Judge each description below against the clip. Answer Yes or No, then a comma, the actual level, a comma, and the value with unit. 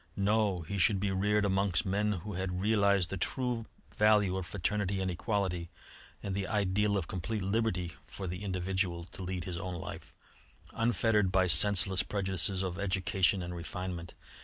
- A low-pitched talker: Yes, very low, 95 Hz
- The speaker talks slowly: No, average, 160 wpm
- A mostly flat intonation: Yes, narrow, 2.1 semitones